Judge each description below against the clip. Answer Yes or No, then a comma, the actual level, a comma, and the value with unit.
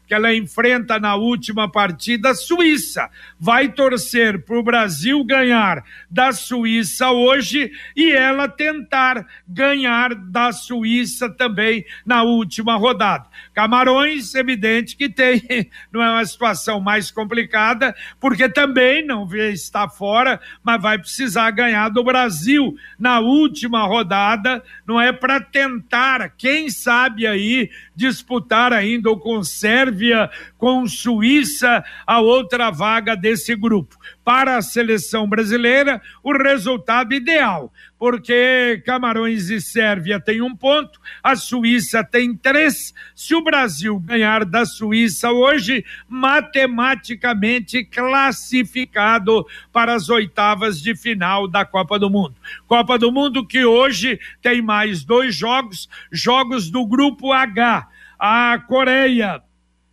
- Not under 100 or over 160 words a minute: Yes, slow, 120 wpm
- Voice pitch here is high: Yes, high, 235 Hz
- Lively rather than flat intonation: No, average, 2.8 semitones